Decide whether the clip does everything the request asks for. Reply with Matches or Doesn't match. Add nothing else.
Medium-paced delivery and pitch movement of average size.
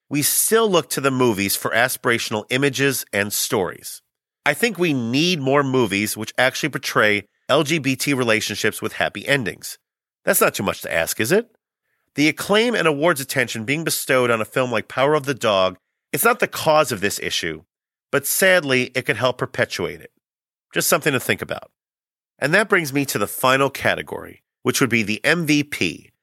Matches